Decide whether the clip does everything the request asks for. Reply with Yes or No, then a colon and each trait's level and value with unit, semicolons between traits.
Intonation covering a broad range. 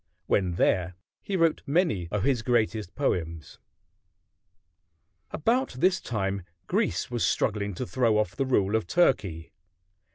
Yes: wide, 6.6 semitones